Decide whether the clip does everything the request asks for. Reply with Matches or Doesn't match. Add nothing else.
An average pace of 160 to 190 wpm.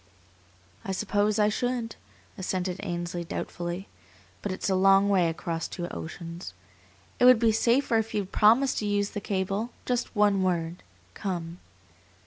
Doesn't match